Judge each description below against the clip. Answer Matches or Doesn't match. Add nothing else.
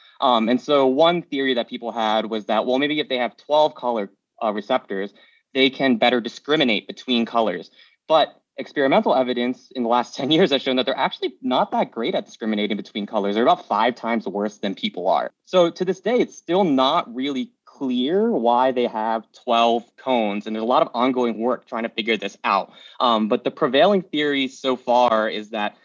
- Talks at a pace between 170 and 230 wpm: Matches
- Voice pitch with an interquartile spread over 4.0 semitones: Doesn't match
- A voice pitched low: Matches